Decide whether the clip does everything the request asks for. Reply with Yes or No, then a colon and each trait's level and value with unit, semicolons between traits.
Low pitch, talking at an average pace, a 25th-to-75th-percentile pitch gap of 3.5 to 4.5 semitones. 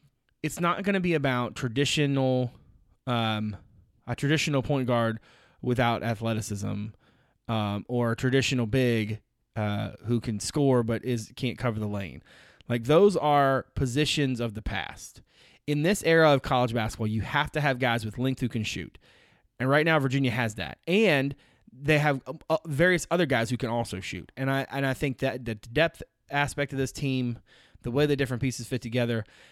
Yes: low, 125 Hz; average, 175 wpm; average, 3.9 semitones